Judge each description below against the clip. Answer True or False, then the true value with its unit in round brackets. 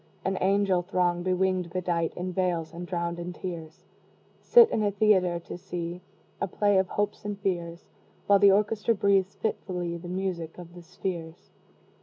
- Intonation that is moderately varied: False (2.1 semitones)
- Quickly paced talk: False (165 wpm)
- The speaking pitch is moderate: True (180 Hz)